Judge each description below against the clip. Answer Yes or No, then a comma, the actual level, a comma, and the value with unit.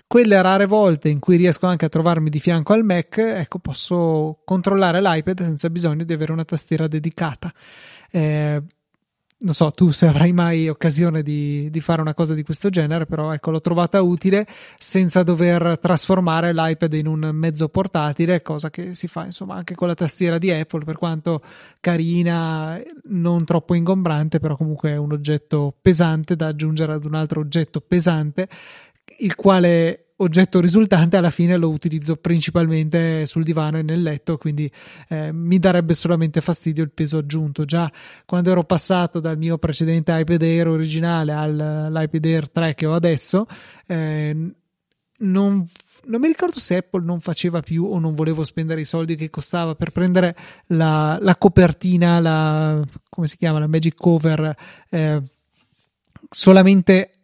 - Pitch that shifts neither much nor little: No, narrow, 2.2 semitones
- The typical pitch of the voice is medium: Yes, medium, 165 Hz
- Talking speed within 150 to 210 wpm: Yes, average, 160 wpm